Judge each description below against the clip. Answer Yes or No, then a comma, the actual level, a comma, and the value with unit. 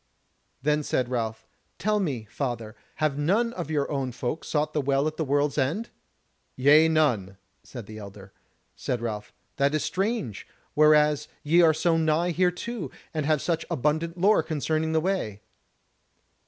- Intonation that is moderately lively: Yes, average, 4.1 semitones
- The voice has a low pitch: No, medium, 150 Hz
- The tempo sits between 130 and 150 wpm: No, average, 160 wpm